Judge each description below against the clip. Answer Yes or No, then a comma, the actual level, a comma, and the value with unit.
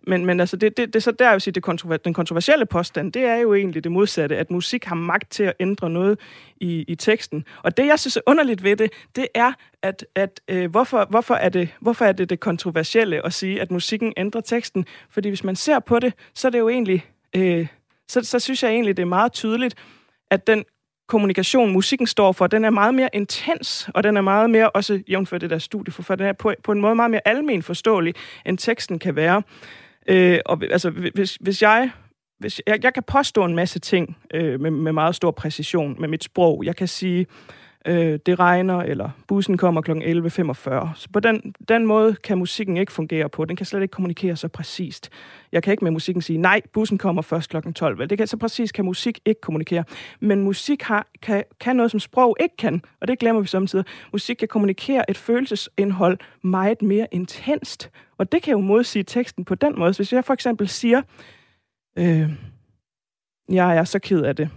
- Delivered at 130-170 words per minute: No, average, 215 wpm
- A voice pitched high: Yes, high, 195 Hz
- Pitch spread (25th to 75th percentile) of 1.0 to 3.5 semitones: No, average, 4.2 semitones